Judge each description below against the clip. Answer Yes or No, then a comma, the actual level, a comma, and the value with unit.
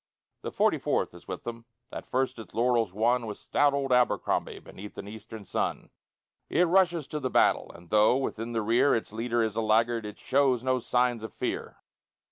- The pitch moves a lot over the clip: No, average, 2.8 semitones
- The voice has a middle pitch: No, low, 120 Hz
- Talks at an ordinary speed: Yes, average, 195 wpm